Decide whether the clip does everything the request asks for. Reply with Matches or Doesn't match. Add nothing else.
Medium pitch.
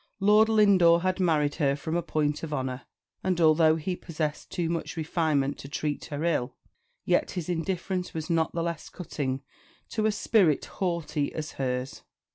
Matches